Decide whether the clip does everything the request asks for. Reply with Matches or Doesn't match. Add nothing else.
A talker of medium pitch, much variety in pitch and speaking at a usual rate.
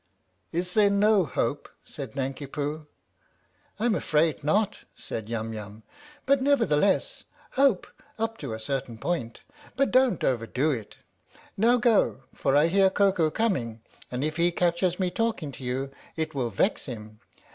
Matches